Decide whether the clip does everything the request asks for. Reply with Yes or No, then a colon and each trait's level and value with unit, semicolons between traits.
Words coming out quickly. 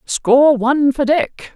No: average, 155 wpm